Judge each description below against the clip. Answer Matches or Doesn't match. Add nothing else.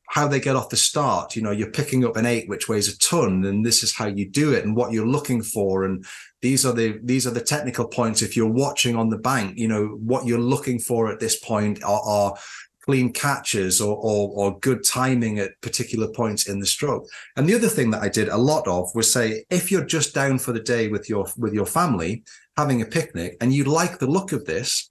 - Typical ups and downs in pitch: Matches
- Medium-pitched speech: Doesn't match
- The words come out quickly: Matches